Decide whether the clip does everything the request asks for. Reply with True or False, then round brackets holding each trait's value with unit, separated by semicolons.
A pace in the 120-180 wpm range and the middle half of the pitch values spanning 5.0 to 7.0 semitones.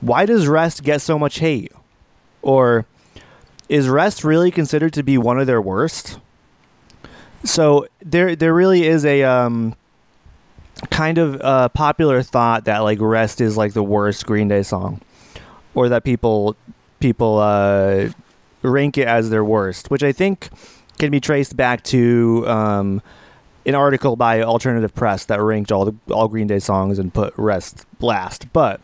True (160 wpm; 5.3 semitones)